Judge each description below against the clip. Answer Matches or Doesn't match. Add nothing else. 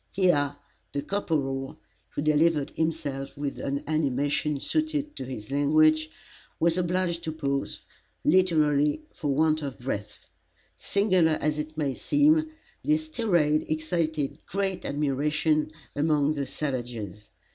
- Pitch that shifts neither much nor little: Matches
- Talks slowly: Matches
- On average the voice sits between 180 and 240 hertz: Doesn't match